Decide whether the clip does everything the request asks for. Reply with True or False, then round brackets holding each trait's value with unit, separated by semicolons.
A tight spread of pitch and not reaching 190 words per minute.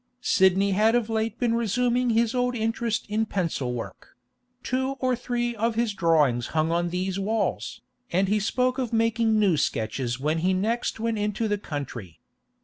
False (5.0 semitones; 170 wpm)